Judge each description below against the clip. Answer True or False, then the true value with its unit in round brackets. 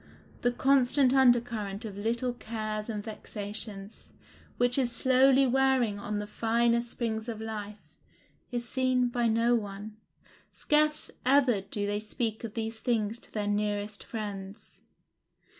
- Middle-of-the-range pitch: False (225 Hz)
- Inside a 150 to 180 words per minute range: False (140 wpm)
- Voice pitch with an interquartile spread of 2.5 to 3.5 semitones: True (2.8 semitones)